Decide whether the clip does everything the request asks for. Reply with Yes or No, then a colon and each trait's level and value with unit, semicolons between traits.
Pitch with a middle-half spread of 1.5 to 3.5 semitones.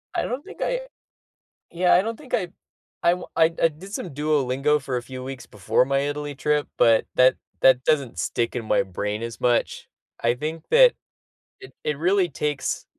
No: average, 5.3 semitones